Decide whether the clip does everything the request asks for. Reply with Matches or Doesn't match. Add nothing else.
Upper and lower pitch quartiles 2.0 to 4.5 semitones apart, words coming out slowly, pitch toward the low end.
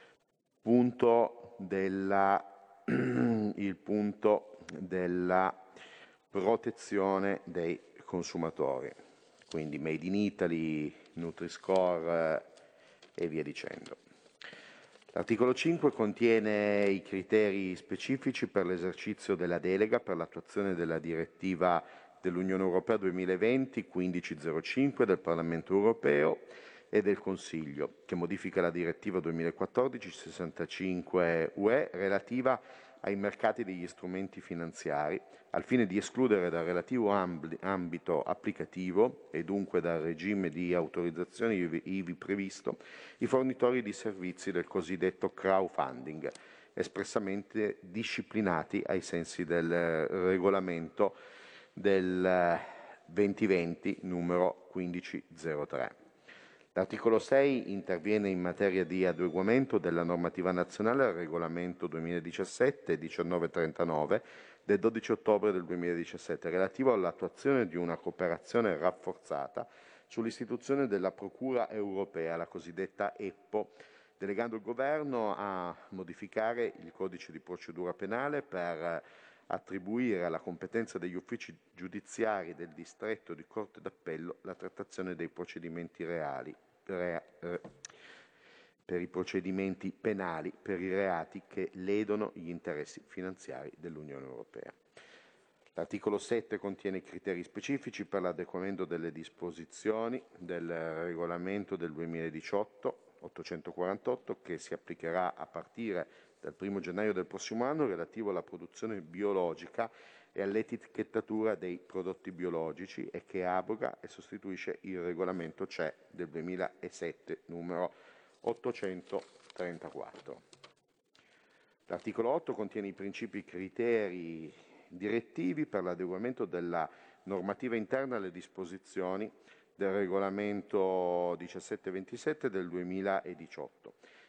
Matches